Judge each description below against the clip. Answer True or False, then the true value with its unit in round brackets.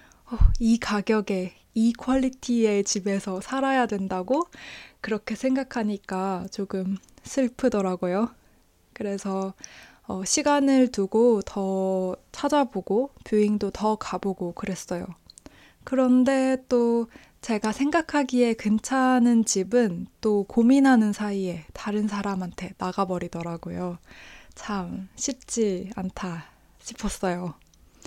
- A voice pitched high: True (210 Hz)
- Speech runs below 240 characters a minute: True (225 characters per minute)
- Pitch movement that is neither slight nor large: True (4.6 semitones)